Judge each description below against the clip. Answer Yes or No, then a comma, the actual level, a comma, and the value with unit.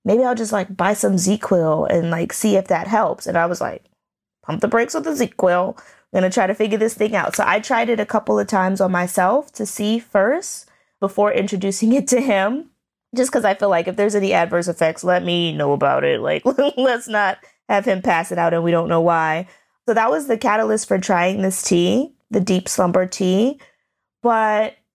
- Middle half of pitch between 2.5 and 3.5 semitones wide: No, average, 4.4 semitones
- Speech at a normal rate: No, fast, 220 wpm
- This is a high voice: Yes, high, 200 Hz